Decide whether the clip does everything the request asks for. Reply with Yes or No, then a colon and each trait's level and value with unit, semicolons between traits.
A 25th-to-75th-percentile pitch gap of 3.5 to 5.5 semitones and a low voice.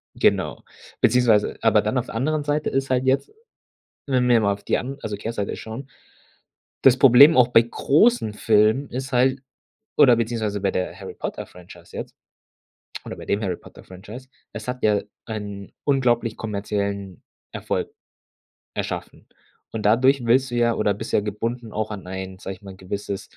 Yes: average, 4.1 semitones; low, 115 Hz